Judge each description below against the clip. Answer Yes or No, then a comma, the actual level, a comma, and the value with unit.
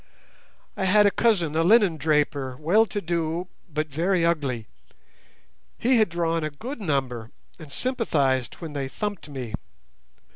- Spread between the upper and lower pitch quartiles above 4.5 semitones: Yes, wide, 5.6 semitones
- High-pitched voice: No, medium, 165 Hz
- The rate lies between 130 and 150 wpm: Yes, average, 145 wpm